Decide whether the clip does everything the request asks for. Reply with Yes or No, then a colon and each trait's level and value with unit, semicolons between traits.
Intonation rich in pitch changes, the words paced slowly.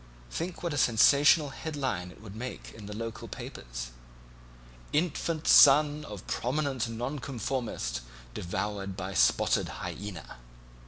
Yes: wide, 6.5 semitones; slow, 115 wpm